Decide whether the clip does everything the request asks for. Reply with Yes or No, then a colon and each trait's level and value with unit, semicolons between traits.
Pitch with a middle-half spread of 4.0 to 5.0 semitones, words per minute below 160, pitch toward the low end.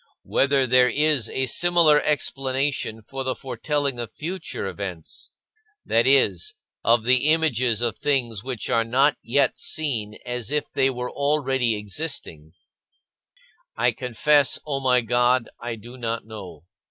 No: average, 3.6 semitones; average, 140 wpm; low, 125 Hz